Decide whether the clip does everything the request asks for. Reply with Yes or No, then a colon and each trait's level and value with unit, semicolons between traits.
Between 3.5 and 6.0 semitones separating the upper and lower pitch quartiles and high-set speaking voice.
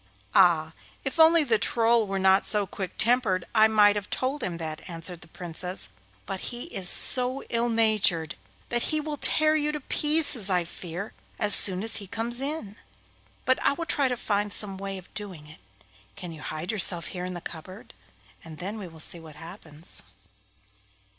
Yes: average, 5.2 semitones; high, 200 Hz